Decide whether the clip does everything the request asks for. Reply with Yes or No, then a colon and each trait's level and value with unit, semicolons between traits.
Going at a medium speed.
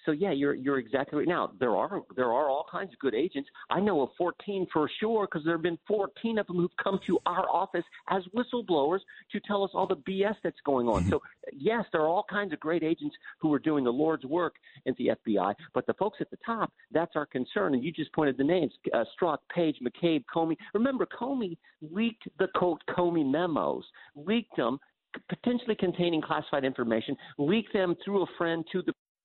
No: fast, 215 wpm